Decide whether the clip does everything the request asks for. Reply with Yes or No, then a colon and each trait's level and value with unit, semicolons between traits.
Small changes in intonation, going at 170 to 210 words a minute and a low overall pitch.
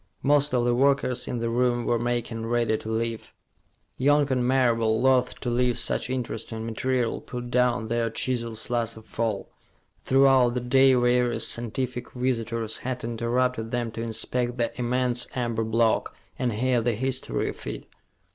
No: narrow, 1.6 semitones; average, 160 wpm; low, 120 Hz